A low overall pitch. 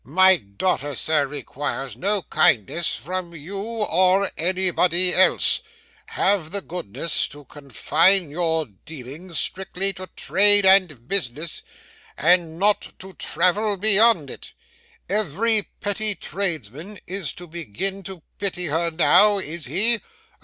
No: medium, 180 Hz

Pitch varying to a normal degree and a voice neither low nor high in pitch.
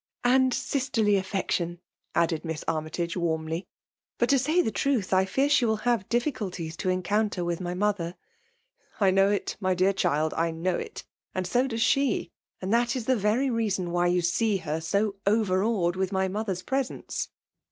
No: average, 4.5 semitones; high, 195 Hz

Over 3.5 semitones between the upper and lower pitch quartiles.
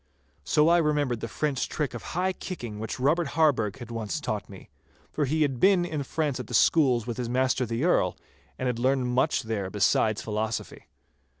Yes: average, 4.9 semitones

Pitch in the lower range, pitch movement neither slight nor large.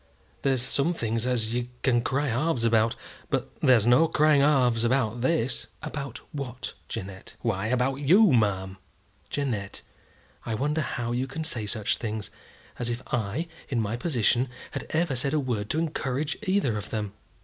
Yes: low, 125 Hz; average, 3.9 semitones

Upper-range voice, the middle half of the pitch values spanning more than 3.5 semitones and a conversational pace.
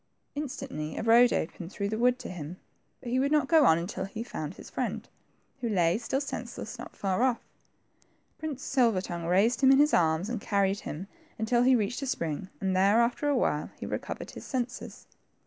No: high, 225 Hz; wide, 5.5 semitones; fast, 210 wpm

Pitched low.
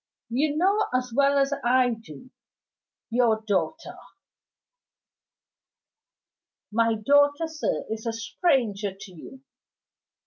No: very high, 250 Hz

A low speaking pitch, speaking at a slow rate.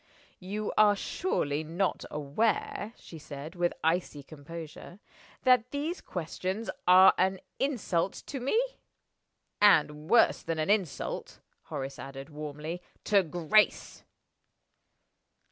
No: medium, 175 Hz; slow, 110 wpm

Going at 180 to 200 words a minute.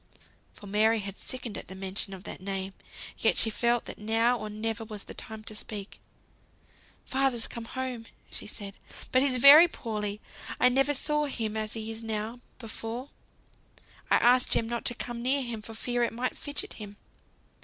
Yes: average, 185 wpm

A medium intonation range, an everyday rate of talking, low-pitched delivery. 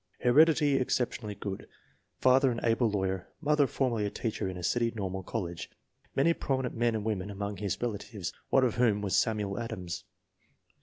Yes: average, 4.1 semitones; average, 170 wpm; low, 110 Hz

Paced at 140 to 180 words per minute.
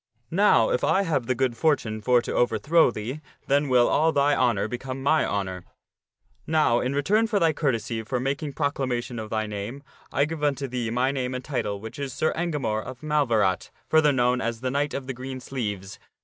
No: average, 200 wpm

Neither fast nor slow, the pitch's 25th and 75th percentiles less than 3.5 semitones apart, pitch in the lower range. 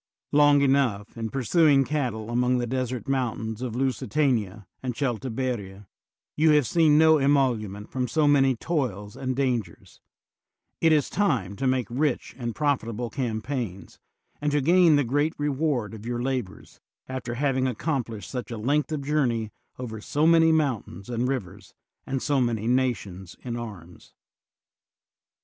No: average, 150 wpm; average, 4.1 semitones; low, 130 Hz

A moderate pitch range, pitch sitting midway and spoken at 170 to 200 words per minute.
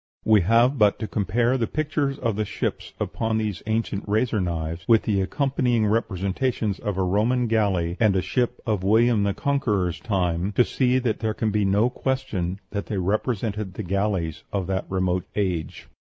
No: average, 3.6 semitones; low, 105 Hz; average, 180 wpm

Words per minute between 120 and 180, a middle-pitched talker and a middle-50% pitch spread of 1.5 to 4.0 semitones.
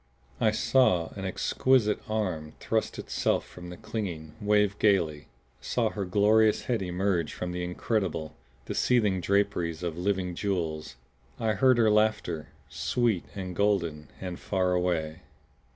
No: slow, 135 wpm; very low, 95 Hz; average, 3.6 semitones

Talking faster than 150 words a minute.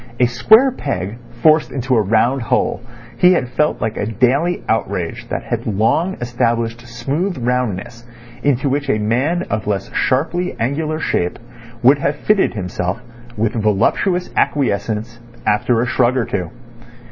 No: average, 145 wpm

